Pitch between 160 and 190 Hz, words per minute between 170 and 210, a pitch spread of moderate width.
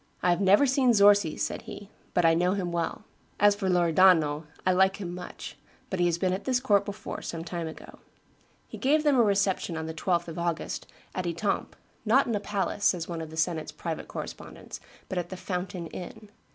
Yes: medium, 185 Hz; fast, 205 wpm; average, 3.0 semitones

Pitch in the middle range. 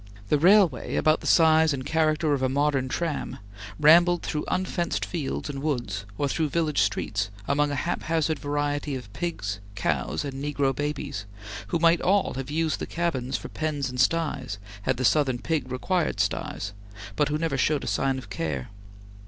Yes: medium, 145 Hz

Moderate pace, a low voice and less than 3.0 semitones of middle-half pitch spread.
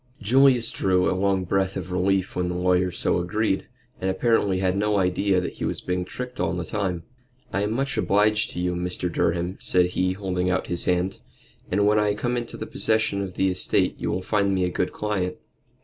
No: fast, 210 wpm; very low, 95 Hz; narrow, 2.4 semitones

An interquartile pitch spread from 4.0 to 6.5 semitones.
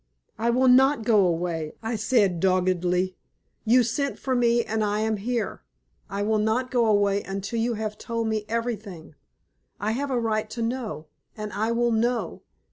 No: average, 2.9 semitones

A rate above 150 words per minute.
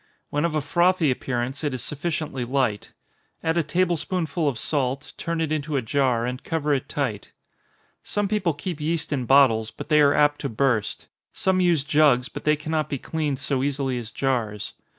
Yes: average, 190 wpm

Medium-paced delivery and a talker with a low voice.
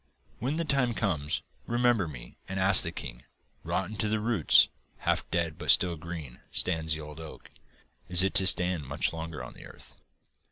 Yes: average, 185 wpm; very low, 90 Hz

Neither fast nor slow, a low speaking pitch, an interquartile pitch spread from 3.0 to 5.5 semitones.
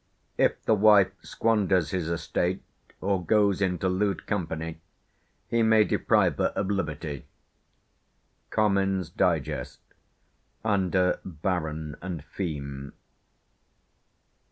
No: slow, 95 wpm; very low, 95 Hz; average, 3.8 semitones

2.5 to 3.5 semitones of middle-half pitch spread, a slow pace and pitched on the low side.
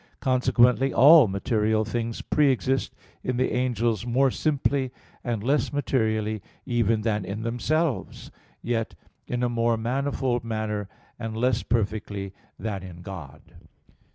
Yes: average, 2.9 semitones; slow, 125 wpm; low, 115 Hz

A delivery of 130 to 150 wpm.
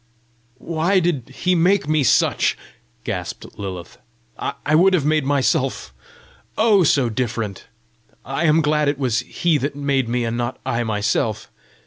Yes: average, 145 wpm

